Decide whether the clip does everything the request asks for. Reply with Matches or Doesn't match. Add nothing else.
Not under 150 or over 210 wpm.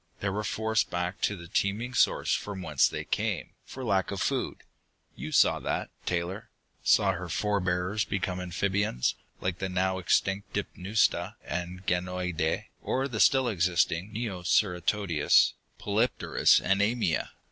Doesn't match